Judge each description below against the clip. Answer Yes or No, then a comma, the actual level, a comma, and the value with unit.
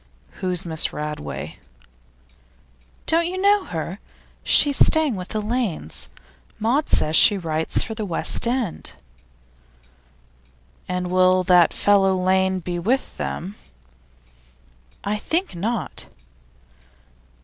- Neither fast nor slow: No, slow, 105 wpm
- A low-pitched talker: No, high, 190 Hz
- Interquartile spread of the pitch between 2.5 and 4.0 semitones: No, average, 5.2 semitones